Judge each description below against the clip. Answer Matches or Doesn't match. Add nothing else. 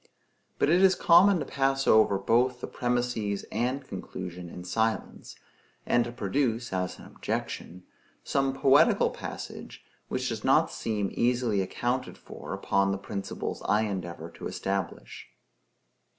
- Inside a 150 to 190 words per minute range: Doesn't match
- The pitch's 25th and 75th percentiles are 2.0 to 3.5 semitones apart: Doesn't match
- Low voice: Matches